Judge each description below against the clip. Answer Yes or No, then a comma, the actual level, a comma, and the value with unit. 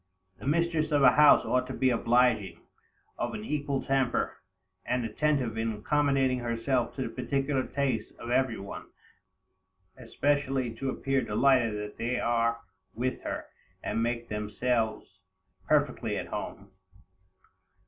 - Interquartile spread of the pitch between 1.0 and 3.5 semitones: Yes, average, 3.1 semitones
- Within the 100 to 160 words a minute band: Yes, slow, 135 wpm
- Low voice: Yes, low, 125 Hz